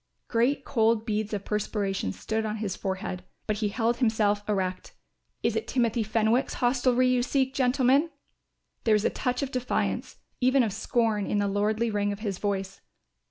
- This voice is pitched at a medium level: No, high, 220 Hz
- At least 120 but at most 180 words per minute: Yes, average, 170 wpm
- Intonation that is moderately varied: Yes, average, 3.3 semitones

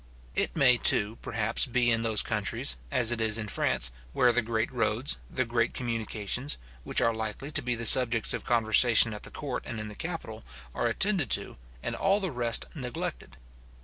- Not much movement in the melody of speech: Yes, narrow, 2.2 semitones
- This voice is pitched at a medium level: No, low, 115 Hz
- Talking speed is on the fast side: No, average, 190 wpm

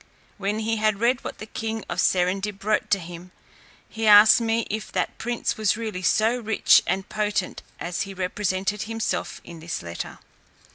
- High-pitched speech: Yes, high, 210 Hz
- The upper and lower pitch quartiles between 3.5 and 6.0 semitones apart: No, average, 2.7 semitones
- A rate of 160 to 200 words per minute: Yes, average, 175 wpm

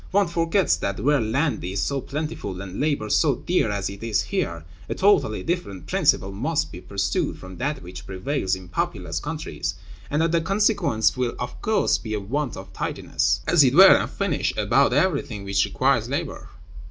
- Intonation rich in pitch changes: Yes, wide, 8.7 semitones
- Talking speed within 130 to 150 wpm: No, average, 185 wpm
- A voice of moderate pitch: No, low, 130 Hz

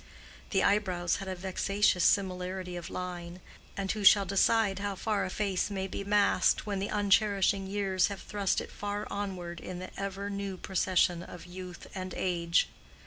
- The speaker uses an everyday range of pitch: No, narrow, 1.8 semitones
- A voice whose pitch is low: No, high, 195 Hz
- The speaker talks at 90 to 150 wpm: No, average, 170 wpm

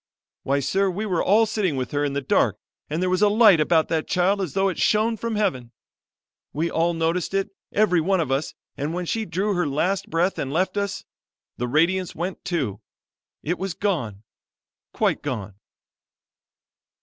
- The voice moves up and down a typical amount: Yes, average, 4.6 semitones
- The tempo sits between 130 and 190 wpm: Yes, average, 185 wpm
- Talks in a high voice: No, medium, 175 Hz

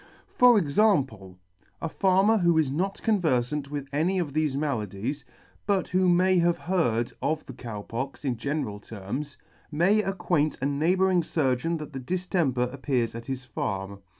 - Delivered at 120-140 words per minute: No, average, 155 wpm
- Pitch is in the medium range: Yes, medium, 150 Hz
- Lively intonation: Yes, wide, 6.2 semitones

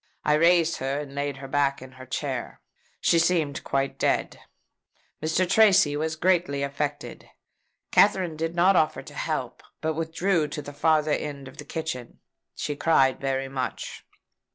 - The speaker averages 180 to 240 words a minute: No, average, 155 wpm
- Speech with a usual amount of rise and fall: Yes, average, 3.0 semitones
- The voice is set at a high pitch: No, medium, 150 Hz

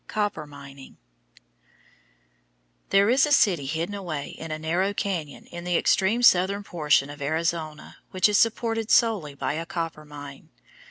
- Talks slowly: No, average, 150 wpm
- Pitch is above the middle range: No, medium, 170 Hz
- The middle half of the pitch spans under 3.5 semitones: No, average, 5.1 semitones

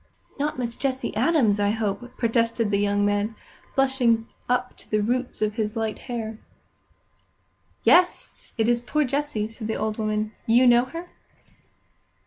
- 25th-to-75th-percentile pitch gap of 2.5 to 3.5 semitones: Yes, average, 2.9 semitones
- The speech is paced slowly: No, average, 150 wpm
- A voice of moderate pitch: No, high, 230 Hz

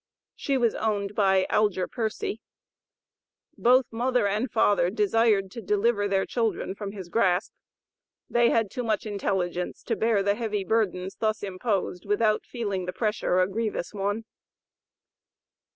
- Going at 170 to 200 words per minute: No, average, 140 wpm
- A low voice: No, high, 210 Hz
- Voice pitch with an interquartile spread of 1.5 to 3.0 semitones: Yes, average, 2.7 semitones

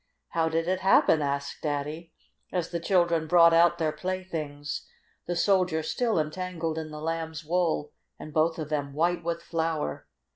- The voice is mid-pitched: Yes, medium, 165 Hz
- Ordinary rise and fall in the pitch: No, narrow, 2.0 semitones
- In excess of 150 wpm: Yes, average, 160 wpm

